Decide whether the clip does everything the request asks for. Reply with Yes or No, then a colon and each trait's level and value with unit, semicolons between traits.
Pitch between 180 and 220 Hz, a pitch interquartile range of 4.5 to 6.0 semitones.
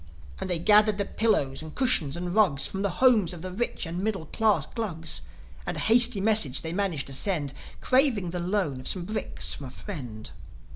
Yes: medium, 185 Hz; average, 5.2 semitones